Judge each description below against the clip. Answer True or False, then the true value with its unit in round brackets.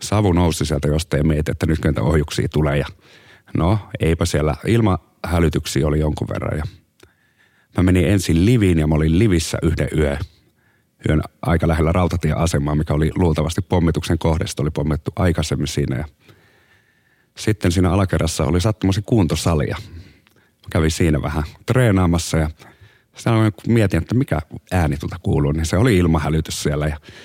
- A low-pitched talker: True (85 Hz)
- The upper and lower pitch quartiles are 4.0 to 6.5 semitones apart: True (4.8 semitones)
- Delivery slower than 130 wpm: False (150 wpm)